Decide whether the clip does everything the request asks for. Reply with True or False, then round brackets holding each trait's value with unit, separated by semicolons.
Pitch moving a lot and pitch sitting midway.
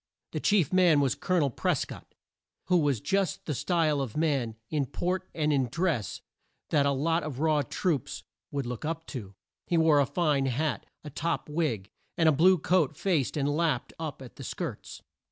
False (3.5 semitones; 150 Hz)